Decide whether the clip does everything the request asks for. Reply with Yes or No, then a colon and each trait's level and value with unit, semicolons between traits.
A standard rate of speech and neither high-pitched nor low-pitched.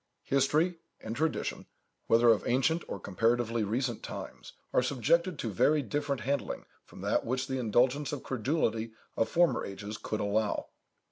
No: average, 150 wpm; low, 125 Hz